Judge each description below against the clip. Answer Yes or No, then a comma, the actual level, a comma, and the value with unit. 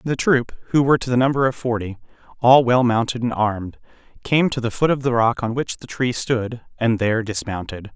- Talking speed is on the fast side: Yes, fast, 220 wpm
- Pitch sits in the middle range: No, low, 120 Hz